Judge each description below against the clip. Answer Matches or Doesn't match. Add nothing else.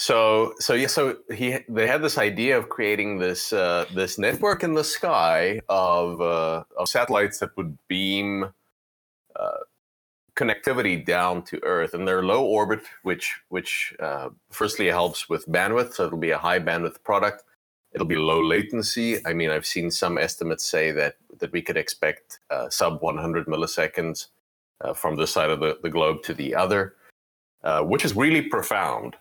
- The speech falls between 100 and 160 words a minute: Doesn't match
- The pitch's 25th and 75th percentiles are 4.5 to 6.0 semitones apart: Matches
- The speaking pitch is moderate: Doesn't match